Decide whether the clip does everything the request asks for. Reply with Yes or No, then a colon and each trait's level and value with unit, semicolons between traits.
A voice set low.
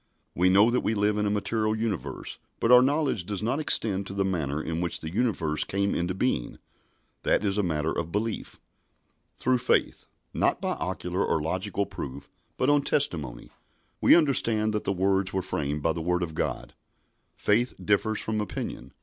Yes: low, 100 Hz